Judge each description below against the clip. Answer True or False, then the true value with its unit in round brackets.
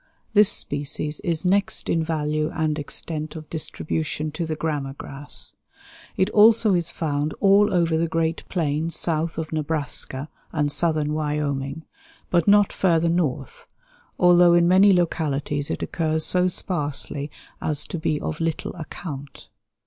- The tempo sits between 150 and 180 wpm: False (140 wpm)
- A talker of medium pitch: True (160 Hz)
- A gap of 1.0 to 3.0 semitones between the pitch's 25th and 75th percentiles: True (2.6 semitones)